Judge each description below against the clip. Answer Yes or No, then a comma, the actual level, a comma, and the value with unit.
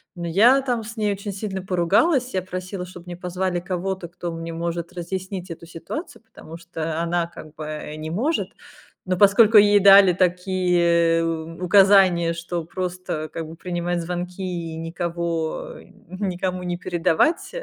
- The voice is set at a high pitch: No, medium, 180 Hz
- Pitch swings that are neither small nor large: No, narrow, 2.2 semitones